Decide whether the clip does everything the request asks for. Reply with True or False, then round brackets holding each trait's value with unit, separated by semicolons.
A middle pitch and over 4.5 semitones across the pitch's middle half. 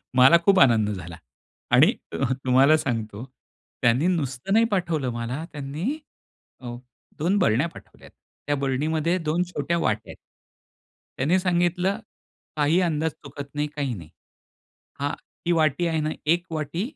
True (150 Hz; 4.9 semitones)